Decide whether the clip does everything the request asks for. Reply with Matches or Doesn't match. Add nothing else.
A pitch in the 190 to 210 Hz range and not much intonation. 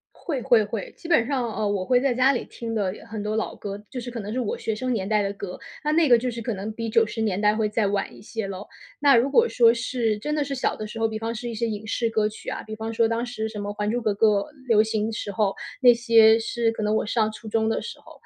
Doesn't match